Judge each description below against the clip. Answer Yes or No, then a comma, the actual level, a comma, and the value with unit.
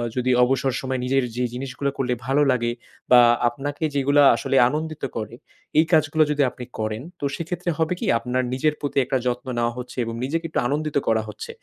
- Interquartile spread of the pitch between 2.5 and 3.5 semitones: Yes, average, 3.2 semitones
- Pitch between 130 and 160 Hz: Yes, low, 135 Hz